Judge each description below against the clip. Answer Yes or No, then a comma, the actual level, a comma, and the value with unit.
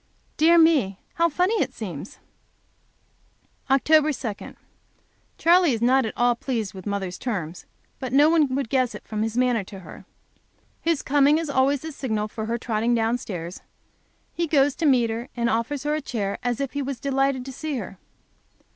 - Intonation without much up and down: No, average, 4.6 semitones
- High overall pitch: Yes, very high, 255 Hz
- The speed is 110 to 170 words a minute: No, average, 180 wpm